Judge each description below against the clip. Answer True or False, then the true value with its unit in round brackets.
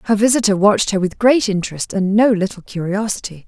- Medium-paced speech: True (190 wpm)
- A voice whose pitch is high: True (205 Hz)